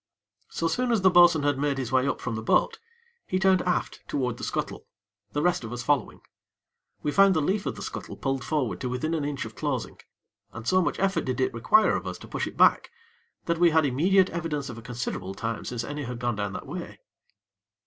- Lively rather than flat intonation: Yes, wide, 5.9 semitones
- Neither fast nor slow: No, fast, 230 wpm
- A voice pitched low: No, medium, 145 Hz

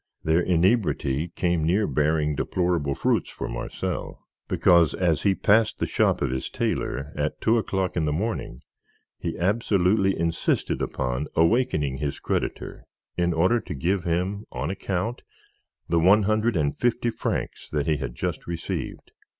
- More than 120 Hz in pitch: No, very low, 85 Hz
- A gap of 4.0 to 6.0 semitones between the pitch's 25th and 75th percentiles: Yes, average, 4.7 semitones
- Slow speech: No, average, 150 wpm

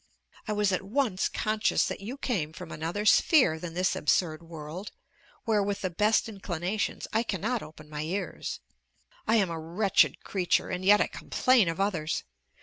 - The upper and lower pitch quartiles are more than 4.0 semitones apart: Yes, average, 4.4 semitones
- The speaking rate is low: No, average, 170 wpm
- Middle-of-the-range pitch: No, high, 195 Hz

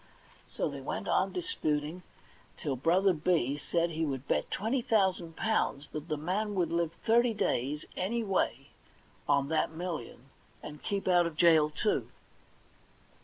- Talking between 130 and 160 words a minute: Yes, average, 150 wpm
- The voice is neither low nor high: Yes, medium, 170 Hz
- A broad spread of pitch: No, average, 4.5 semitones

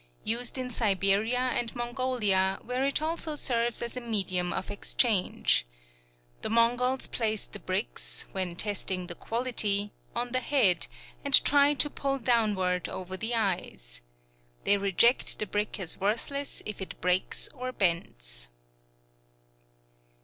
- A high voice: Yes, high, 220 Hz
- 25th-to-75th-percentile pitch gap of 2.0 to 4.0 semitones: No, average, 4.9 semitones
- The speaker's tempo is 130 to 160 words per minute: Yes, slow, 135 wpm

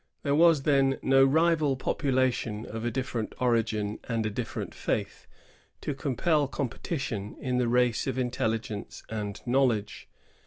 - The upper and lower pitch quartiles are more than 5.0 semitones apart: No, average, 3.4 semitones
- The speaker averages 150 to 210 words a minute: No, average, 140 wpm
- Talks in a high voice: No, low, 125 Hz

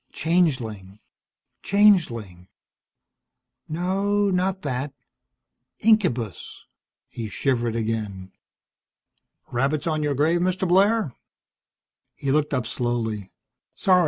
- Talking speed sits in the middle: No, slow, 85 wpm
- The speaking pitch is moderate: Yes, medium, 145 Hz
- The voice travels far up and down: Yes, wide, 8.0 semitones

